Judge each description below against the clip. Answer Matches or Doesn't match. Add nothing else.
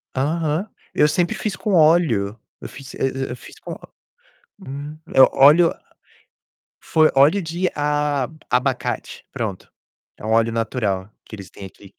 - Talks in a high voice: Doesn't match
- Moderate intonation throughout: Matches